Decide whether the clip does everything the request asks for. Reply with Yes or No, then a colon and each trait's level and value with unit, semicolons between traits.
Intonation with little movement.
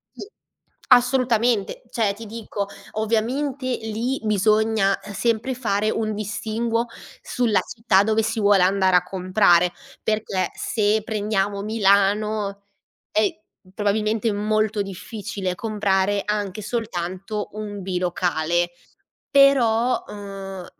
Yes: narrow, 2.2 semitones